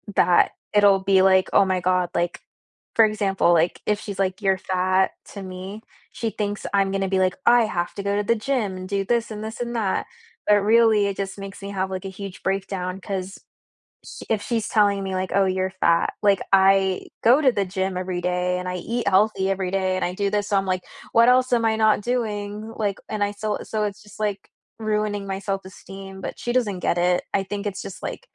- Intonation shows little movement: Yes, narrow, 2.0 semitones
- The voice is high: Yes, high, 195 Hz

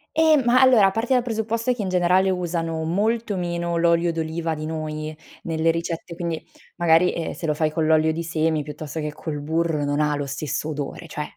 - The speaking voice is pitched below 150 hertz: No, medium, 165 Hz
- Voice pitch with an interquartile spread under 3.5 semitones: Yes, average, 2.8 semitones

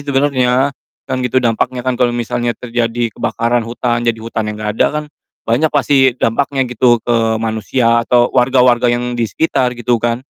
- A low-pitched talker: Yes, low, 120 Hz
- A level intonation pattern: Yes, narrow, 1.6 semitones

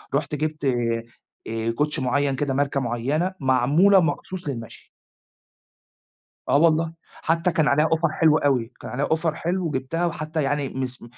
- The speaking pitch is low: No, medium, 150 Hz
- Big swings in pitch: No, average, 3.6 semitones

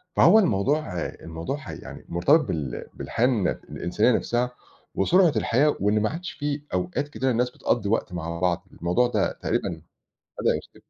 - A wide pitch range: Yes, wide, 8.1 semitones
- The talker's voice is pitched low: Yes, low, 115 Hz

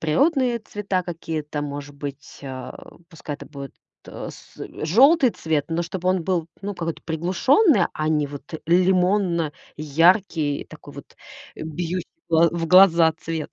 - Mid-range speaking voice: Yes, medium, 165 Hz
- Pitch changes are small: No, average, 3.4 semitones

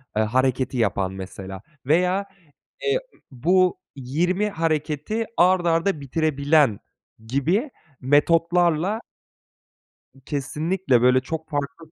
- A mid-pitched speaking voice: Yes, medium, 155 Hz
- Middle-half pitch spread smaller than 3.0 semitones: No, wide, 5.4 semitones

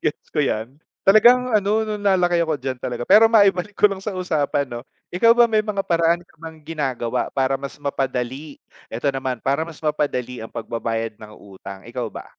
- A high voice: No, medium, 150 Hz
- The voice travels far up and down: Yes, wide, 7.0 semitones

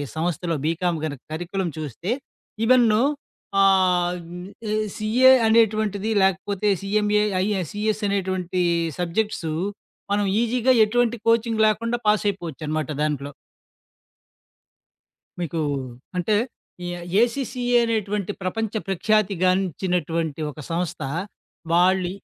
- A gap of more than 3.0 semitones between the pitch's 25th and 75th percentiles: Yes, average, 3.7 semitones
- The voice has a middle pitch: No, high, 195 Hz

